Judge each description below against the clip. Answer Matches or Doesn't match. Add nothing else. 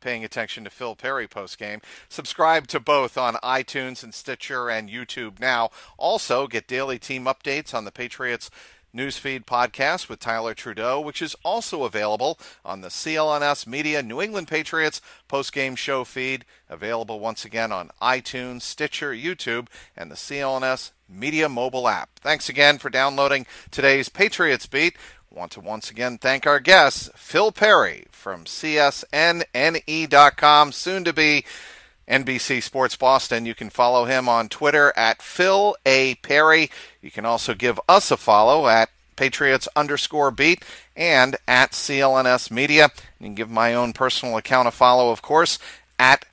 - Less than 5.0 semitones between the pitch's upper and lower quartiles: Matches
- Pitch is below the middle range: Matches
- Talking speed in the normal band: Matches